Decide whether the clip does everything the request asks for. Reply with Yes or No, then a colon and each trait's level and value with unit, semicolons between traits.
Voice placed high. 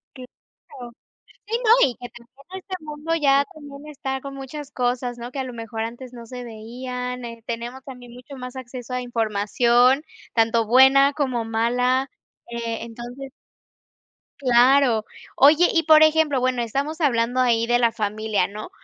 Yes: very high, 250 Hz